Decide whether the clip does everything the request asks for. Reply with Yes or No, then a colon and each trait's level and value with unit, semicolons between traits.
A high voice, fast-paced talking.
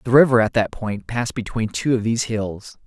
No: low, 115 Hz; fast, 230 wpm